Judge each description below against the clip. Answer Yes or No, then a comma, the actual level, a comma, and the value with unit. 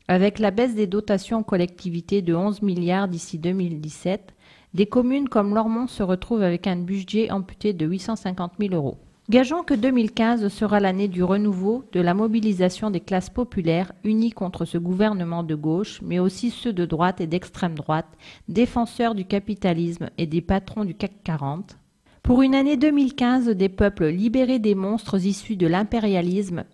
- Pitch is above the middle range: Yes, high, 200 Hz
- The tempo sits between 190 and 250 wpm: No, average, 165 wpm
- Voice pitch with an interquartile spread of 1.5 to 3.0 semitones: No, average, 3.8 semitones